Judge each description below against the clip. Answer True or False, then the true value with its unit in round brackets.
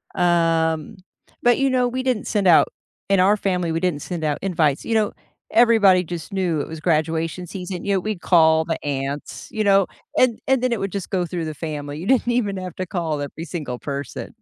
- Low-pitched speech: False (180 Hz)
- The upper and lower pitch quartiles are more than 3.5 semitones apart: True (4.0 semitones)